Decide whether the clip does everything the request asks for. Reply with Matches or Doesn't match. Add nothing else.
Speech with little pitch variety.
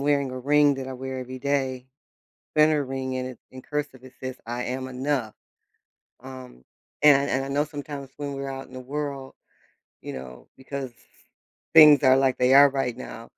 Matches